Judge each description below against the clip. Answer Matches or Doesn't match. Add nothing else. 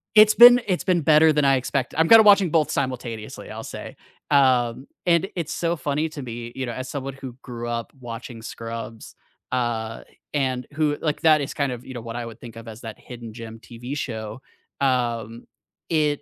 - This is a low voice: Matches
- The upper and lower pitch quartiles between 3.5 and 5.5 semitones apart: Matches